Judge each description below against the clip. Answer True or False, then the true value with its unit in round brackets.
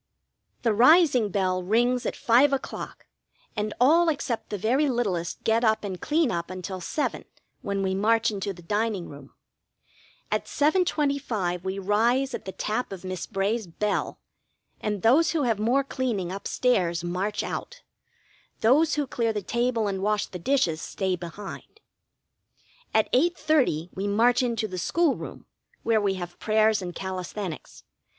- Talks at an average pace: True (155 wpm)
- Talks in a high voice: True (215 Hz)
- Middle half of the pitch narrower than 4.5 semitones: False (4.8 semitones)